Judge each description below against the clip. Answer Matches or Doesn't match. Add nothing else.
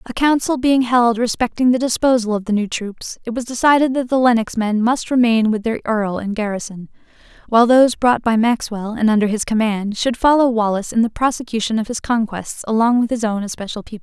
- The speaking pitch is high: Matches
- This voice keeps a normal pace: Doesn't match